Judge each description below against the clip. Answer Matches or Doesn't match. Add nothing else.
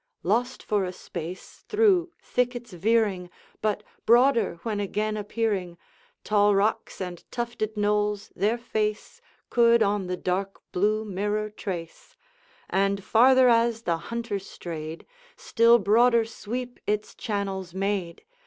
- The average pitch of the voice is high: Matches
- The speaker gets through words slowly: Matches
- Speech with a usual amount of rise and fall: Matches